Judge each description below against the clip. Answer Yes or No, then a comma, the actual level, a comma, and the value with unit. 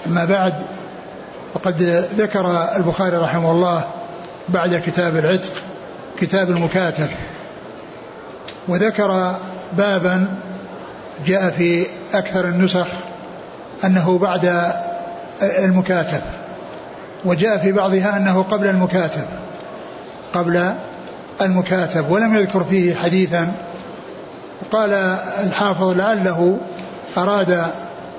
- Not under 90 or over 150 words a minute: No, average, 80 wpm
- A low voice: No, medium, 185 Hz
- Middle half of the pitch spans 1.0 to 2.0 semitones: Yes, narrow, 1.7 semitones